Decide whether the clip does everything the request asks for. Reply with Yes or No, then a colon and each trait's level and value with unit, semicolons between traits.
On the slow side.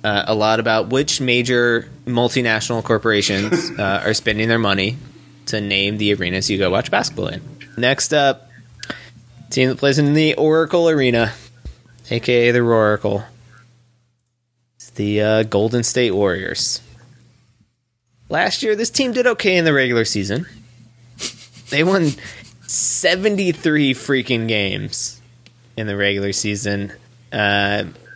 Yes: slow, 130 wpm